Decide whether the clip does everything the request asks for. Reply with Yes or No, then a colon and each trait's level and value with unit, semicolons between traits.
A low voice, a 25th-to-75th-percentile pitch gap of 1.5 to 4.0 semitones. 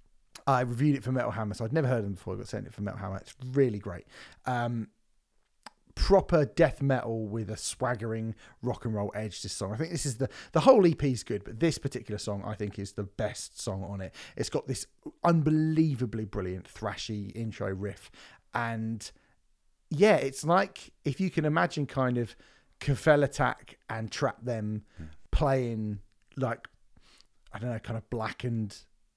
No: low, 115 Hz; average, 4.7 semitones